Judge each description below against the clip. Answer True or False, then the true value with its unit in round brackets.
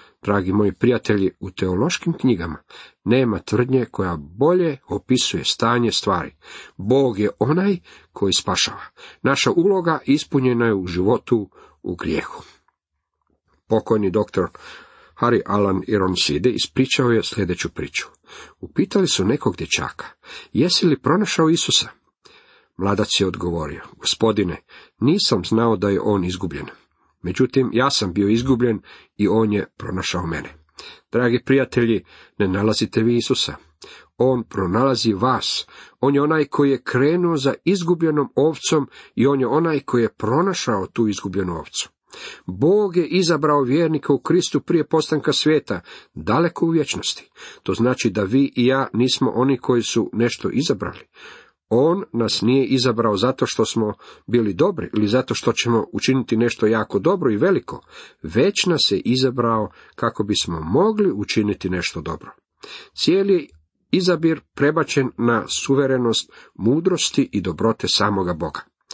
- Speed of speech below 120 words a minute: False (135 wpm)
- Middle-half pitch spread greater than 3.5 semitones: True (5.4 semitones)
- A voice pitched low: True (120 Hz)